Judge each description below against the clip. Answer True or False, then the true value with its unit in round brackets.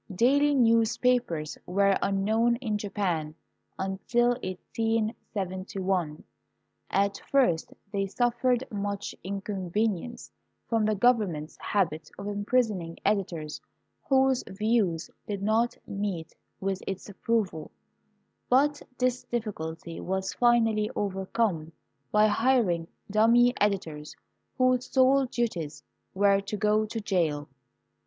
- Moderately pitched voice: False (205 Hz)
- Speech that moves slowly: True (105 wpm)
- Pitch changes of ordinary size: True (4.0 semitones)